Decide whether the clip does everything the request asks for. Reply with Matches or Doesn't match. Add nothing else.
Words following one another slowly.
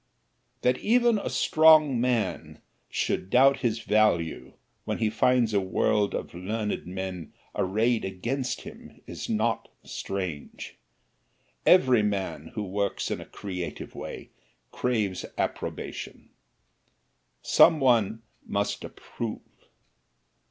Matches